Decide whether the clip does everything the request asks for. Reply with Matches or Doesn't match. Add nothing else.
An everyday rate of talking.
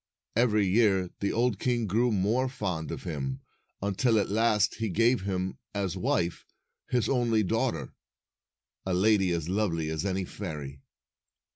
Matches